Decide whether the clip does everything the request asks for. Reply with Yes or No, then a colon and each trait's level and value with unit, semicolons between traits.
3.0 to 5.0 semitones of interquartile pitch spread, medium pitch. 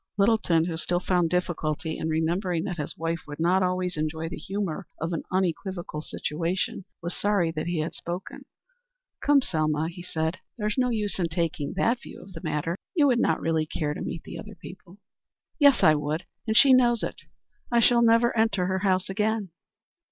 Yes: average, 4.3 semitones; medium, 180 Hz